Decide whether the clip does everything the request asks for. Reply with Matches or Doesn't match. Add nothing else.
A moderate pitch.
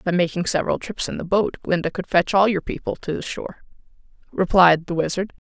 Matches